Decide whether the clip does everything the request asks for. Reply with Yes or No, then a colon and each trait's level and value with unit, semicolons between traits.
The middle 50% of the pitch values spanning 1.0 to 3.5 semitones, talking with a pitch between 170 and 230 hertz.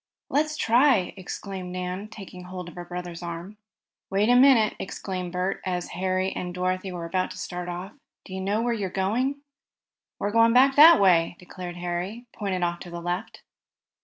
Yes: average, 3.2 semitones; medium, 185 Hz